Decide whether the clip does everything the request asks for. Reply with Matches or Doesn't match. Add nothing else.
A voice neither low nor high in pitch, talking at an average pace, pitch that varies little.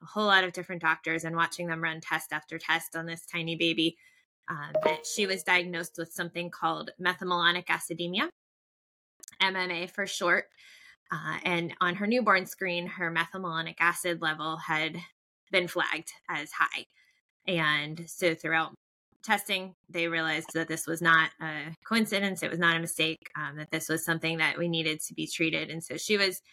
Matches